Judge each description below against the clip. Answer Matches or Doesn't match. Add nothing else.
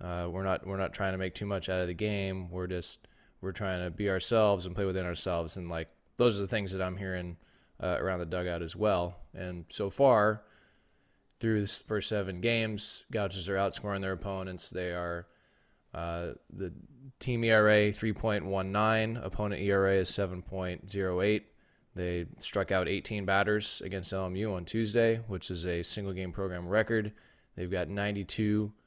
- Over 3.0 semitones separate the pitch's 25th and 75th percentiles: Doesn't match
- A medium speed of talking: Matches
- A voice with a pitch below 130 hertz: Matches